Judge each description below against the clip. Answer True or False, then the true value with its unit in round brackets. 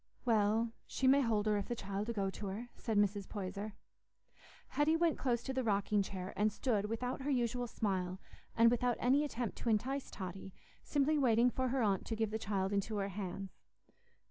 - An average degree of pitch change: True (3.8 semitones)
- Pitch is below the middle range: False (220 Hz)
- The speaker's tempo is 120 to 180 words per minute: False (195 wpm)